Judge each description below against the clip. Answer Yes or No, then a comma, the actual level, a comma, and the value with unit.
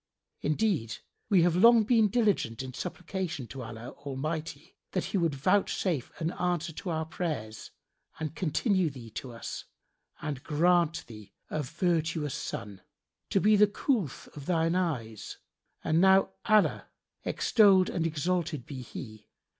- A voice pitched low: No, medium, 165 Hz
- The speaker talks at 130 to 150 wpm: Yes, average, 145 wpm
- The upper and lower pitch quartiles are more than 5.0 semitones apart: Yes, wide, 5.5 semitones